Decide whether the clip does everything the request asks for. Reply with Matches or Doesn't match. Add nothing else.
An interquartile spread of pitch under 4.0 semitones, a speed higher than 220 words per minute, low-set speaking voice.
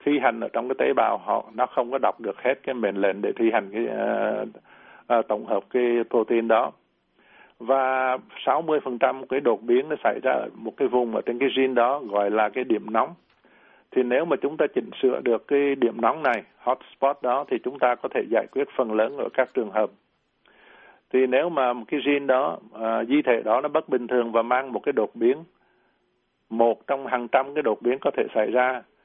Matches